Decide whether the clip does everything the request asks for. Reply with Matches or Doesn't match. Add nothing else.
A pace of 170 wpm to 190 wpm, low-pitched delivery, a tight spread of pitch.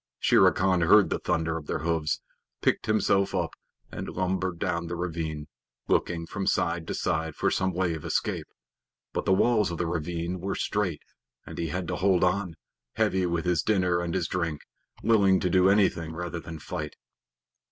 Matches